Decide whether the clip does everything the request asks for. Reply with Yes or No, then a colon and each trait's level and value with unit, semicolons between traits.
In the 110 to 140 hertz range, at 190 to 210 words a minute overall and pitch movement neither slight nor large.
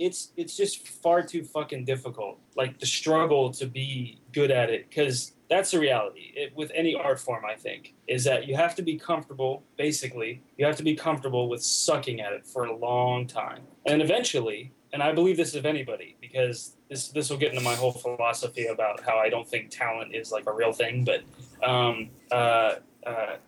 Yes: low, 135 Hz; average, 200 wpm; average, 3.8 semitones